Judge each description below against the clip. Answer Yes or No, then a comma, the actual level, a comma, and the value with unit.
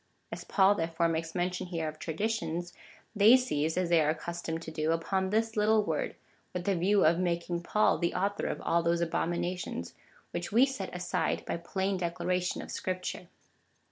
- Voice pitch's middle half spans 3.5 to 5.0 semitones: No, narrow, 2.6 semitones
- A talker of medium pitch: Yes, medium, 175 Hz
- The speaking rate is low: No, average, 180 wpm